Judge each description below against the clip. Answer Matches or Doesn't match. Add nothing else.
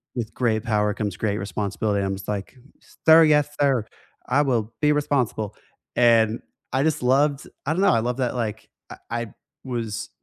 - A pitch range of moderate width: Matches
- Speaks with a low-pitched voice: Matches